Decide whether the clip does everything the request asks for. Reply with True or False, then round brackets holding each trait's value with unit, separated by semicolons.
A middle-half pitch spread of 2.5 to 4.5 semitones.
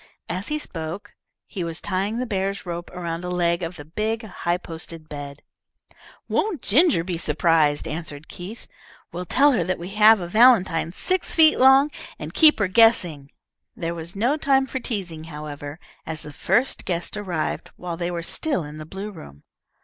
False (5.1 semitones)